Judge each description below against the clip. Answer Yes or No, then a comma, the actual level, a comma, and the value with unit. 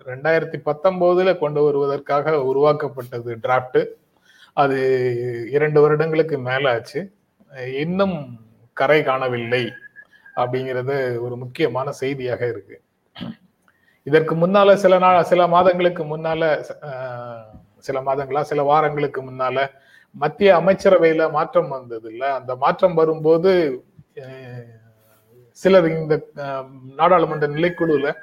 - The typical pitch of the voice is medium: Yes, medium, 145 Hz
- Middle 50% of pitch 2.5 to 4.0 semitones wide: No, average, 4.5 semitones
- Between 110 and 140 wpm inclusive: No, average, 90 wpm